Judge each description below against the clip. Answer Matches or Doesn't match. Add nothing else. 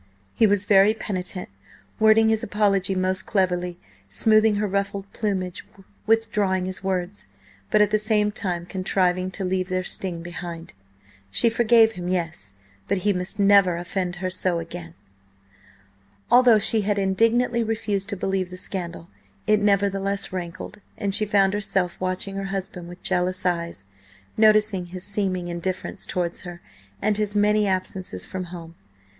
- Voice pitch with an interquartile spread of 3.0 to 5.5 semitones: Doesn't match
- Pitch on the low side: Doesn't match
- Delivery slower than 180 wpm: Matches